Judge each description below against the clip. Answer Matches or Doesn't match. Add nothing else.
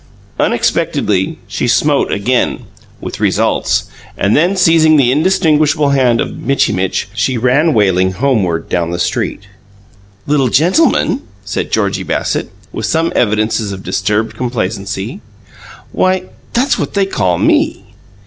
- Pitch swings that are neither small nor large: Doesn't match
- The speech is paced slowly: Matches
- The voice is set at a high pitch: Doesn't match